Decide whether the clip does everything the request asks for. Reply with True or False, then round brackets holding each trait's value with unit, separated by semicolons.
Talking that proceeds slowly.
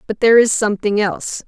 False (205 wpm)